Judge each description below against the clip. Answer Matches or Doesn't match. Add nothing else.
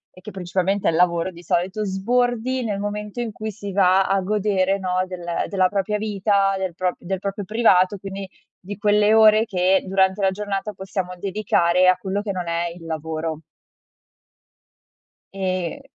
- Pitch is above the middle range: Matches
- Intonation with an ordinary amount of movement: Doesn't match